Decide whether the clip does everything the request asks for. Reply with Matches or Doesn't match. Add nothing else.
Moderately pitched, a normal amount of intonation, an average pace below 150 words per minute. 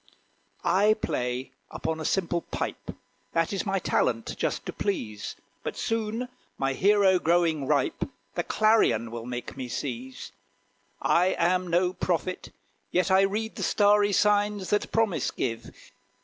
Doesn't match